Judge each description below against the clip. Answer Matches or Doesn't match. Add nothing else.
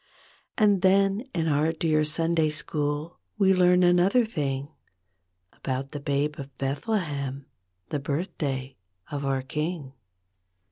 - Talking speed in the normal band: Doesn't match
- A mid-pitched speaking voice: Matches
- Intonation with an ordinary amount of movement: Matches